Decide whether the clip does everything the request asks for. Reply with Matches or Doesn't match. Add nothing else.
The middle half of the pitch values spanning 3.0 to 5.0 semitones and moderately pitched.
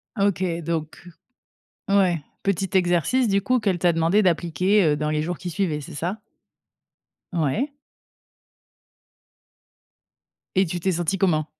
Matches